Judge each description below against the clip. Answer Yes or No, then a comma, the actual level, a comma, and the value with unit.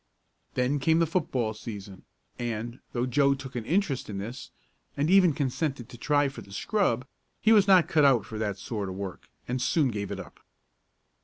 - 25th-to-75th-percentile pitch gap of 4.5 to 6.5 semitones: Yes, average, 5.3 semitones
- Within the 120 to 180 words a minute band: No, average, 190 wpm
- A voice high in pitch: No, low, 130 Hz